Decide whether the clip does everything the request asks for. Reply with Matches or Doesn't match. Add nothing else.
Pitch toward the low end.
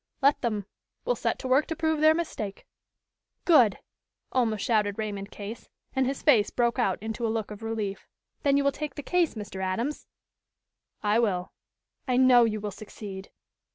Doesn't match